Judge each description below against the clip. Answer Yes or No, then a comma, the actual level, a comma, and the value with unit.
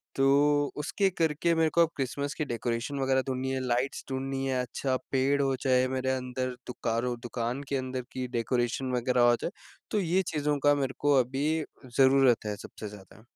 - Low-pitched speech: Yes, low, 130 Hz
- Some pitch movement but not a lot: No, narrow, 2.3 semitones